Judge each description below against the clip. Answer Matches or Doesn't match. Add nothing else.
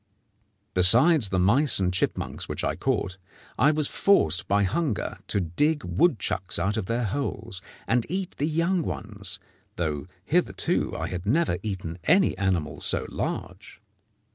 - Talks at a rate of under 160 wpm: Matches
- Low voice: Matches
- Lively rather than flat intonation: Matches